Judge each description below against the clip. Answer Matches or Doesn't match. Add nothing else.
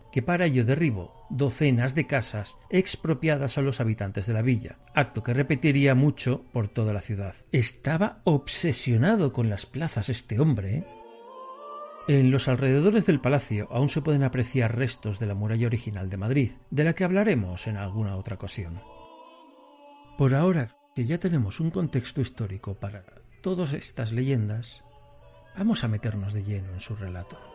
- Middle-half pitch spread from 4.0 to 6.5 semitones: Matches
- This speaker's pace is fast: Doesn't match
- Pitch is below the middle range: Matches